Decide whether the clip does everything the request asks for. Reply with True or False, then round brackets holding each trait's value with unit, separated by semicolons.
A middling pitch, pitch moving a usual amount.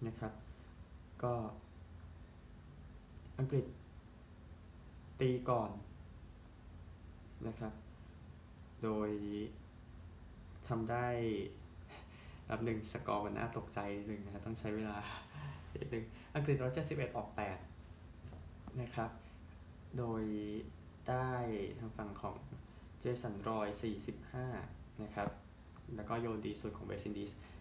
False (105 Hz; 4.9 semitones)